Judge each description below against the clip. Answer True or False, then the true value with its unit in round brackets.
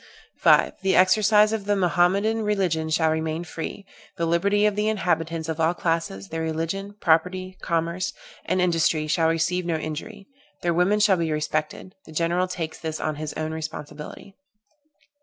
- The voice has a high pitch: False (170 Hz)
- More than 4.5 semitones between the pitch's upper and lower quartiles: False (3.2 semitones)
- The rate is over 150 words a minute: True (160 wpm)